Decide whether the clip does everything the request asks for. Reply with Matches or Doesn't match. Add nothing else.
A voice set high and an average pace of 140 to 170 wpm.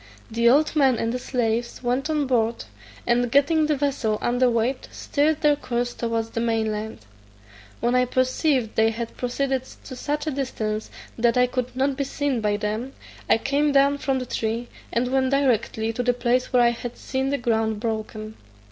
Doesn't match